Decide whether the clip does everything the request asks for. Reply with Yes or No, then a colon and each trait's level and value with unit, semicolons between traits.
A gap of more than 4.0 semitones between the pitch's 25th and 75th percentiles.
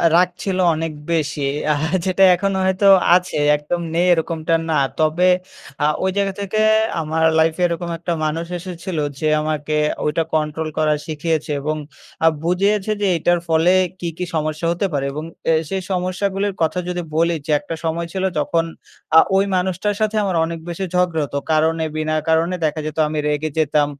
No: average, 2.8 semitones